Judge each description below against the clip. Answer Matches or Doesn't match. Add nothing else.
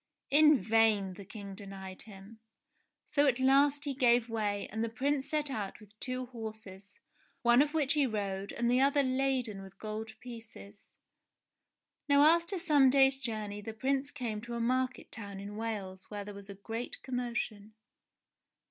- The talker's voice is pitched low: Doesn't match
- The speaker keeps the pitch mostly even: Doesn't match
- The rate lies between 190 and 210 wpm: Doesn't match